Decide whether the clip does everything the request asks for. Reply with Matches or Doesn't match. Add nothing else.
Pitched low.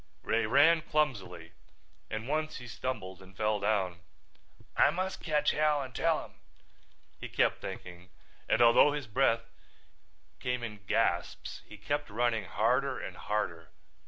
Matches